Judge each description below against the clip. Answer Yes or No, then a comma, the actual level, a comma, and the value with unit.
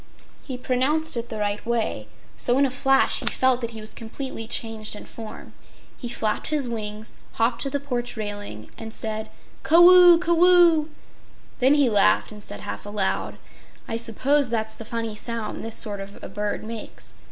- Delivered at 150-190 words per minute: Yes, average, 185 wpm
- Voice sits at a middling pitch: No, high, 230 Hz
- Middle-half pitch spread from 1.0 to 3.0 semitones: No, average, 4.0 semitones